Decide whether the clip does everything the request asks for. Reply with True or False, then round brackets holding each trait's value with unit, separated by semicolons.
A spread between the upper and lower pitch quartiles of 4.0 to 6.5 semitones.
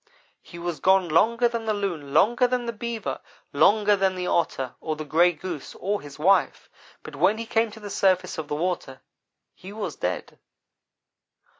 True (4.9 semitones)